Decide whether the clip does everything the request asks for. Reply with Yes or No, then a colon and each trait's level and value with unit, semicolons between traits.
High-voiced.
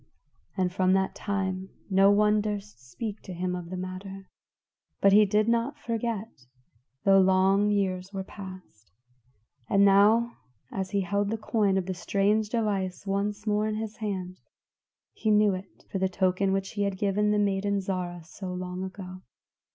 Yes: high, 195 Hz